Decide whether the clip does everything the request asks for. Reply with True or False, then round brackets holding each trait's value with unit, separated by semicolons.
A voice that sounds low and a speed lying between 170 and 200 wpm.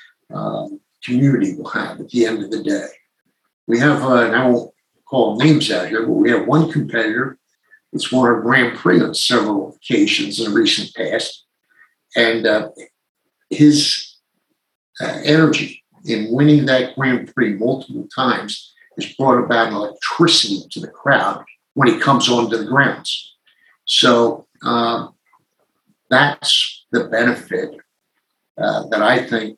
False (130 Hz; 145 wpm)